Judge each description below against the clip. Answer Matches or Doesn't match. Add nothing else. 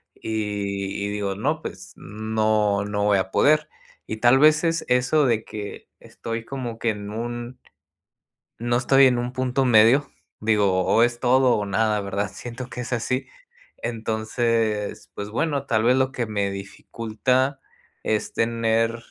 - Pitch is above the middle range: Doesn't match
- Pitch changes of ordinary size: Matches